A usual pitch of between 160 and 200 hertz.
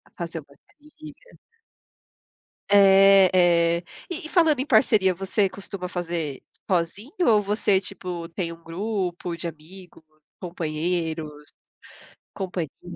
Yes: medium, 185 Hz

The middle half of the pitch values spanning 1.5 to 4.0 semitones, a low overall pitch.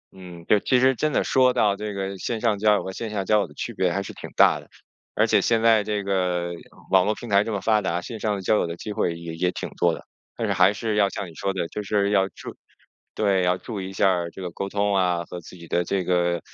Yes: average, 2.9 semitones; low, 100 Hz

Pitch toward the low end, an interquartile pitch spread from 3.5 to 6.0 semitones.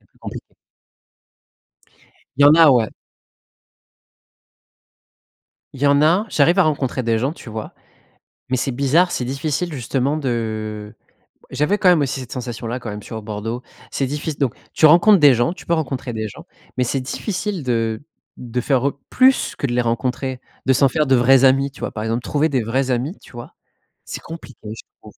Yes: low, 130 Hz; average, 4.0 semitones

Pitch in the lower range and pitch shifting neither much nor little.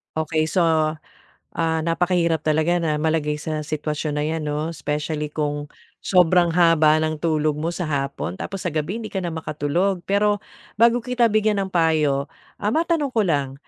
No: medium, 160 Hz; average, 3.3 semitones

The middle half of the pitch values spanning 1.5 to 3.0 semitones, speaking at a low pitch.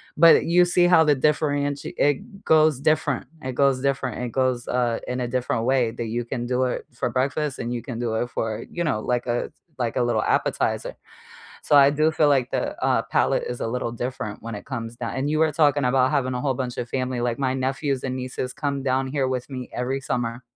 Yes: average, 2.7 semitones; low, 130 Hz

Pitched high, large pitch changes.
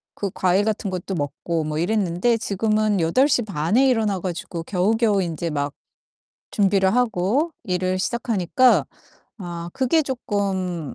No: high, 195 Hz; average, 4.3 semitones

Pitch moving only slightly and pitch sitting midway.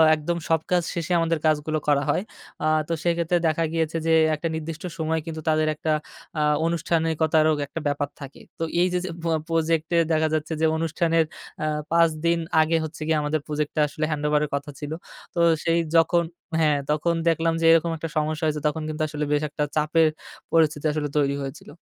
Yes: narrow, 1.5 semitones; medium, 160 Hz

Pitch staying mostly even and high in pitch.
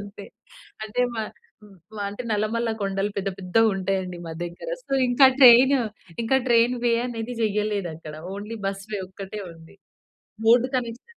No: average, 3.3 semitones; high, 210 Hz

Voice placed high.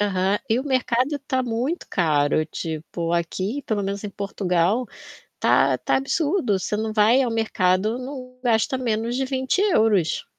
Yes: high, 220 Hz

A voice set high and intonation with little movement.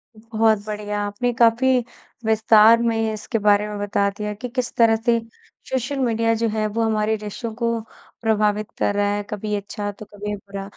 Yes: high, 215 Hz; narrow, 1.7 semitones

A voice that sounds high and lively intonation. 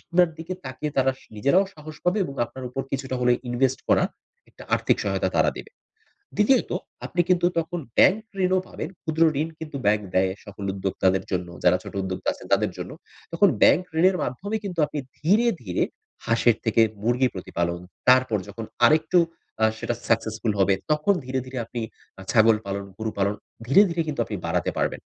No: low, 130 Hz; wide, 7.4 semitones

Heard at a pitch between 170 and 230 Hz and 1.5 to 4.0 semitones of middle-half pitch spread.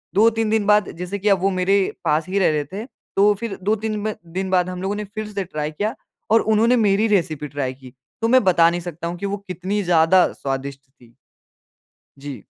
No: high, 190 Hz; average, 4.6 semitones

